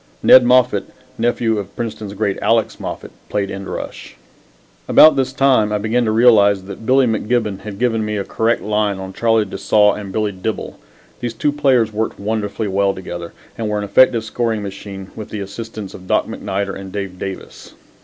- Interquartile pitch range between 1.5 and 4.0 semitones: Yes, narrow, 2.5 semitones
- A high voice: No, low, 105 Hz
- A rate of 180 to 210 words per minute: Yes, average, 185 wpm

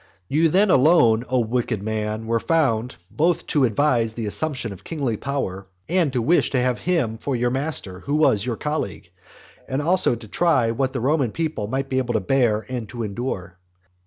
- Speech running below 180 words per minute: No, average, 190 wpm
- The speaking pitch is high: No, low, 125 Hz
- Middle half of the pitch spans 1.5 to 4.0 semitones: No, average, 4.9 semitones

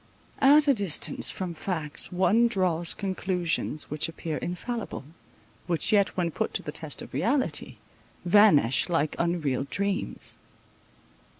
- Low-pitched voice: No, medium, 175 Hz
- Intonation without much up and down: No, average, 4.2 semitones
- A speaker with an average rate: No, slow, 125 wpm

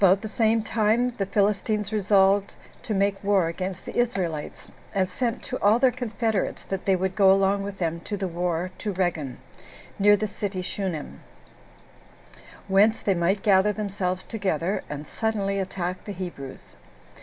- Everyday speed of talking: Yes, average, 165 wpm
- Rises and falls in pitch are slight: Yes, narrow, 2.3 semitones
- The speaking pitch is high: Yes, high, 195 Hz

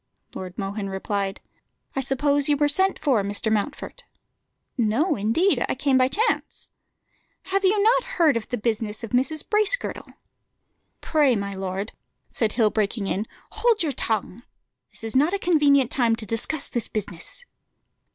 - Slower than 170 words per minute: Yes, average, 155 wpm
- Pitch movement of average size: No, wide, 6.8 semitones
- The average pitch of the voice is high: Yes, very high, 250 Hz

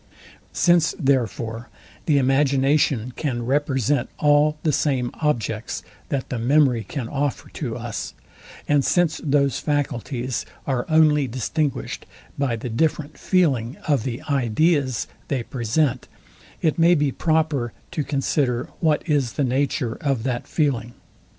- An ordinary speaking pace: No, slow, 130 wpm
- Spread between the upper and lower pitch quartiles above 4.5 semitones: No, average, 3.4 semitones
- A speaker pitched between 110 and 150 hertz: Yes, medium, 140 Hz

